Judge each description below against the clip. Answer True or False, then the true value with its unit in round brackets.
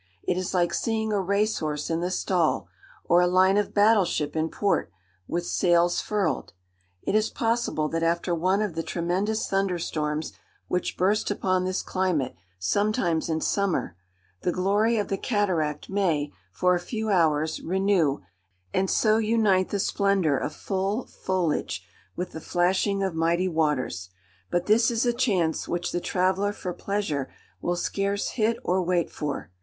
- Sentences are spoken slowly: False (165 wpm)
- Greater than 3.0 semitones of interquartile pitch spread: True (3.4 semitones)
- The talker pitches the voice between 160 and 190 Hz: True (185 Hz)